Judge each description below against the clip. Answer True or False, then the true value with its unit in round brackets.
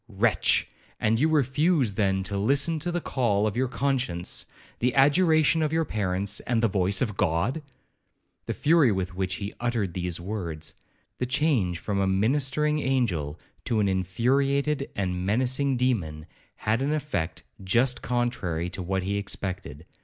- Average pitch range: False (6.3 semitones)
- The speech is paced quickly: False (155 wpm)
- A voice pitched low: True (110 Hz)